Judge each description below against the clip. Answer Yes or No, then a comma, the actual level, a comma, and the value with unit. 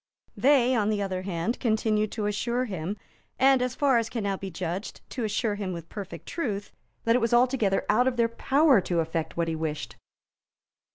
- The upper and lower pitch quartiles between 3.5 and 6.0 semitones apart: Yes, average, 4.5 semitones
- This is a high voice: Yes, high, 215 Hz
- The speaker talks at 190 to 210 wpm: Yes, average, 195 wpm